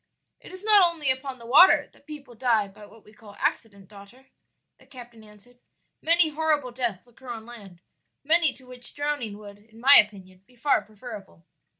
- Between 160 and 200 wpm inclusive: Yes, average, 185 wpm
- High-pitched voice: Yes, high, 240 Hz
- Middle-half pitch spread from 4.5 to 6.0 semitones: Yes, average, 5.1 semitones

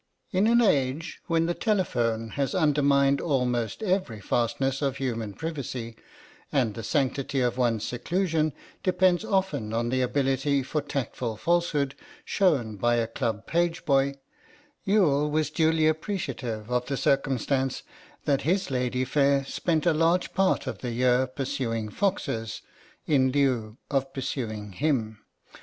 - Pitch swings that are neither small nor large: Yes, average, 4.8 semitones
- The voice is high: No, low, 135 Hz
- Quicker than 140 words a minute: No, slow, 135 wpm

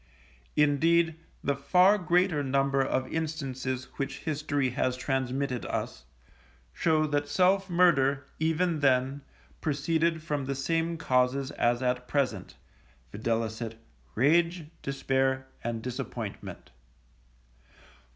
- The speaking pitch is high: No, medium, 140 Hz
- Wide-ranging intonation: No, average, 3.7 semitones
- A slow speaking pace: Yes, slow, 100 wpm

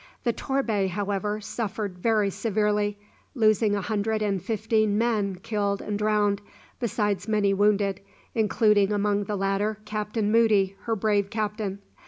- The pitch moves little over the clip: Yes, narrow, 1.3 semitones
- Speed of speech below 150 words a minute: Yes, slow, 135 wpm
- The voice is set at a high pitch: Yes, high, 210 Hz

